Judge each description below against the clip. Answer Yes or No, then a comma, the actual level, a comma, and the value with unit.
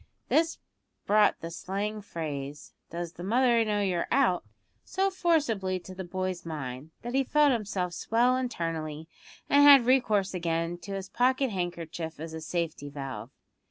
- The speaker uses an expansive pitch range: Yes, wide, 6.4 semitones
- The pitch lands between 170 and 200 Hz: Yes, medium, 185 Hz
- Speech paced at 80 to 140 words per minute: No, average, 155 wpm